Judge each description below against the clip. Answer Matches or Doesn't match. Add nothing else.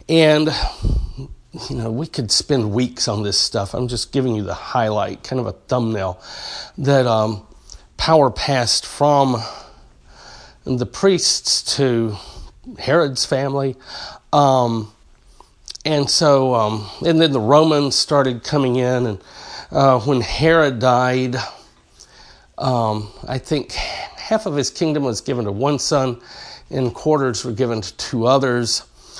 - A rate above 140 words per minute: Doesn't match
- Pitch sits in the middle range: Doesn't match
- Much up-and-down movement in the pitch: Doesn't match